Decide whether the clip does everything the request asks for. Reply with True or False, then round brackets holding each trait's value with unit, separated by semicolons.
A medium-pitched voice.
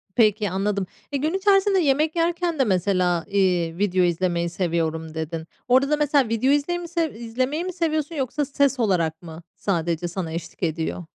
False (210 Hz)